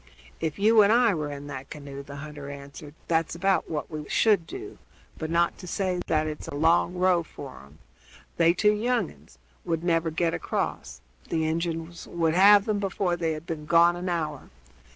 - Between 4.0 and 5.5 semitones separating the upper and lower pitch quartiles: No, average, 3.3 semitones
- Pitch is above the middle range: No, medium, 165 Hz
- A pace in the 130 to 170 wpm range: No, average, 195 wpm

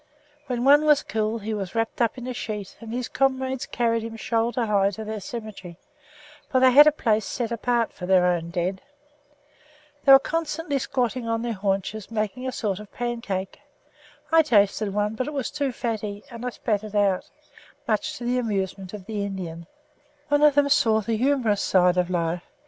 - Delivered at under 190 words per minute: No, average, 195 wpm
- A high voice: Yes, high, 225 Hz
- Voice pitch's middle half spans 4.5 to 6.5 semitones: No, average, 4.0 semitones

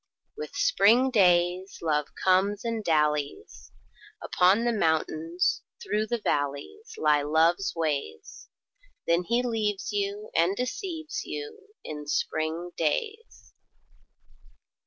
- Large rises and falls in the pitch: Yes, wide, 6.8 semitones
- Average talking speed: No, slow, 105 wpm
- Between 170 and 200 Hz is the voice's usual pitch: Yes, high, 190 Hz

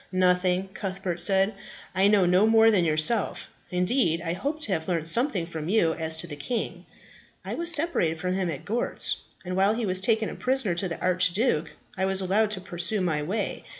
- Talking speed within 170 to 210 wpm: Yes, average, 200 wpm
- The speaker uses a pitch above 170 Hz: Yes, medium, 185 Hz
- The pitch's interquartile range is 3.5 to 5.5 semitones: Yes, average, 4.0 semitones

